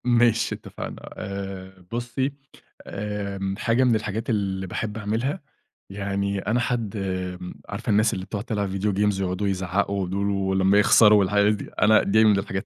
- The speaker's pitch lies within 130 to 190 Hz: No, low, 100 Hz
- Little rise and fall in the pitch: Yes, narrow, 2.1 semitones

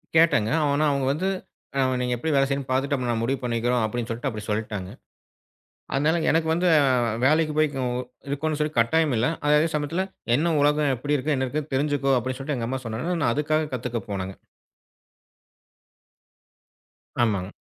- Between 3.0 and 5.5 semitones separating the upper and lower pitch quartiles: Yes, average, 4.1 semitones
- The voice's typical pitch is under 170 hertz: Yes, medium, 140 Hz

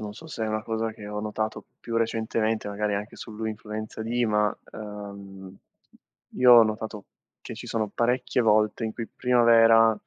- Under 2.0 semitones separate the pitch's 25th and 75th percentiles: Yes, narrow, 1.3 semitones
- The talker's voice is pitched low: Yes, low, 110 Hz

